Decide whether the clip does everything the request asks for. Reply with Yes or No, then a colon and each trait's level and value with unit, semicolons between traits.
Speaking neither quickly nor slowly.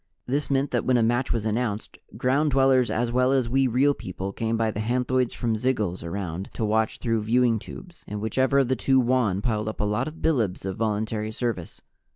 No: fast, 210 wpm